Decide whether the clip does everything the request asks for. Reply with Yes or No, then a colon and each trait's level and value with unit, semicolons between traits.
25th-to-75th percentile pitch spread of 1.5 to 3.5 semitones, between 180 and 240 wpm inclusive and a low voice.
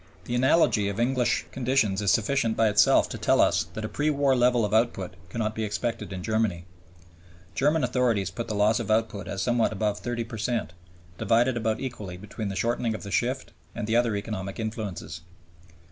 Yes: average, 2.8 semitones; average, 190 wpm; low, 110 Hz